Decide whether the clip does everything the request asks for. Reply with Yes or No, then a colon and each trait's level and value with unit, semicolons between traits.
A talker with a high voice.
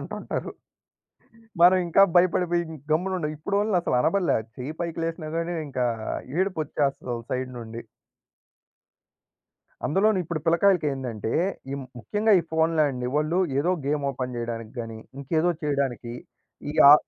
No: medium, 155 Hz